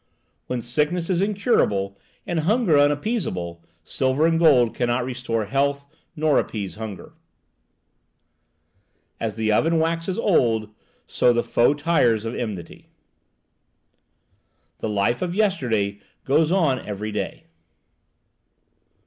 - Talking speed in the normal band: No, slow, 110 wpm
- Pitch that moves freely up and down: Yes, wide, 7.0 semitones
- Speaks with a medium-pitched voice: No, low, 130 Hz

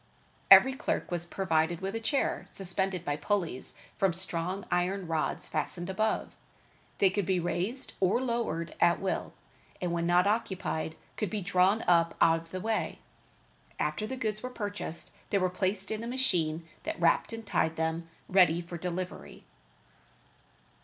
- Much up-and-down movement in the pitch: No, average, 3.3 semitones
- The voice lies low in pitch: No, medium, 185 Hz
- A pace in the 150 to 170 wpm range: Yes, average, 160 wpm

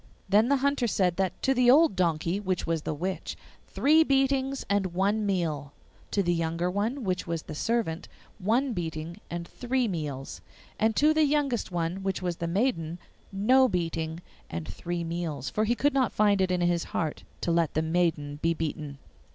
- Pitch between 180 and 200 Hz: Yes, medium, 185 Hz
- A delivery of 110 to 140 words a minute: No, average, 185 wpm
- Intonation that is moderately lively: No, wide, 6.1 semitones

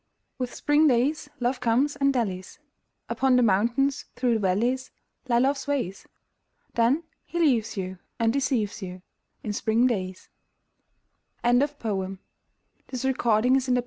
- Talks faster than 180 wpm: No, average, 145 wpm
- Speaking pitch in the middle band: No, high, 245 Hz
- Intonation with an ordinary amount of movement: Yes, average, 3.9 semitones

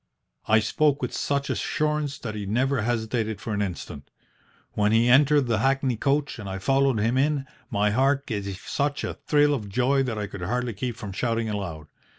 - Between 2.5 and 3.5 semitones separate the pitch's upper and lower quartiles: No, average, 4.8 semitones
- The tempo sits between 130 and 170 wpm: No, average, 190 wpm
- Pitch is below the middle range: Yes, low, 120 Hz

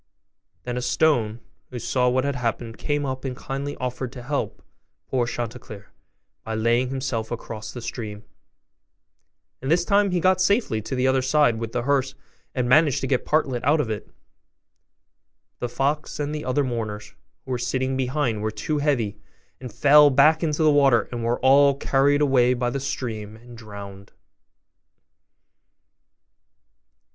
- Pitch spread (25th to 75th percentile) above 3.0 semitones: Yes, average, 3.4 semitones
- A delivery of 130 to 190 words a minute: Yes, average, 165 wpm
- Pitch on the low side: Yes, low, 130 Hz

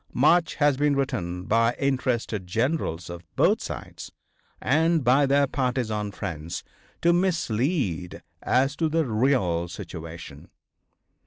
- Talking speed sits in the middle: No, slow, 115 wpm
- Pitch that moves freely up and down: Yes, wide, 8.1 semitones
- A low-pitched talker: Yes, low, 125 Hz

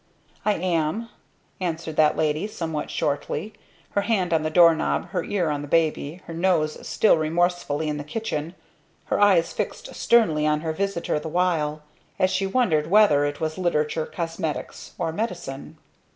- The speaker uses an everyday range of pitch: Yes, average, 3.3 semitones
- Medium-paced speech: Yes, average, 160 wpm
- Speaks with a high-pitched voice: No, medium, 165 Hz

